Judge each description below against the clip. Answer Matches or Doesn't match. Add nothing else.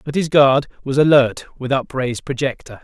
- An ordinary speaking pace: Matches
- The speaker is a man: Matches